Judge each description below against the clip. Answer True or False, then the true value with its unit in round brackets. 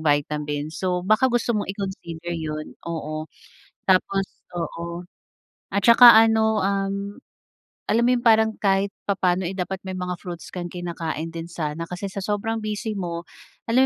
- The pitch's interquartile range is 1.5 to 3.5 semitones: False (3.9 semitones)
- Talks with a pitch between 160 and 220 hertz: True (185 Hz)